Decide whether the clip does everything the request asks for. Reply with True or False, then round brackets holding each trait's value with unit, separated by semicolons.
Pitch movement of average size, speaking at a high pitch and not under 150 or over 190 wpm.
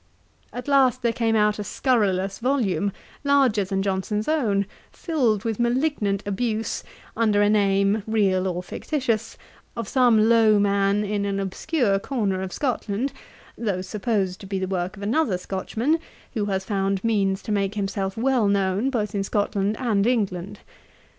True (3.0 semitones; 210 Hz; 155 wpm)